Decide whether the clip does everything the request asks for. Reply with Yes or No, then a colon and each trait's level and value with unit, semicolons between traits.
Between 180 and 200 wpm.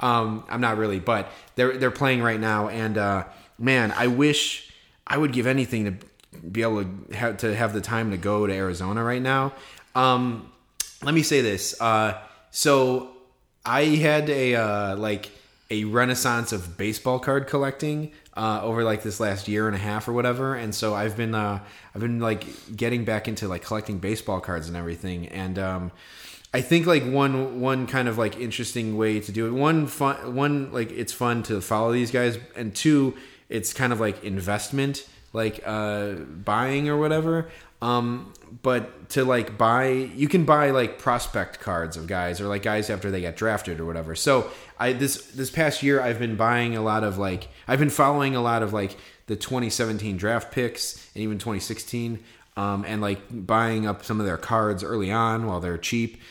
Yes: average, 190 wpm